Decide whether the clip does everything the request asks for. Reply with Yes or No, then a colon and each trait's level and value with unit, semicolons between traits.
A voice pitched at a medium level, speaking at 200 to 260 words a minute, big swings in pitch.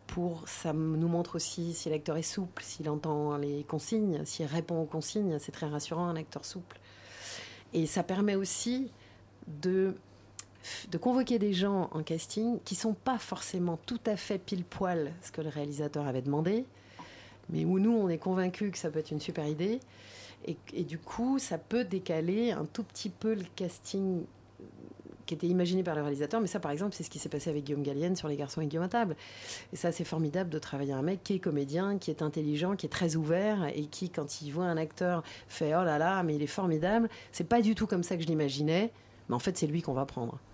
No: medium, 170 Hz; fast, 220 wpm; average, 4.2 semitones